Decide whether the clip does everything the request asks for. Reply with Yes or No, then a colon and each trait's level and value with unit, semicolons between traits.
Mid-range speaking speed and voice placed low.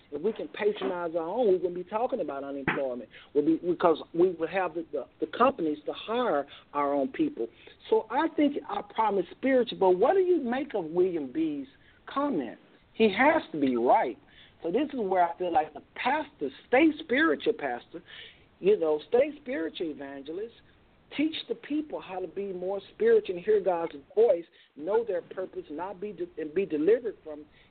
No: average, 190 wpm; high, 245 Hz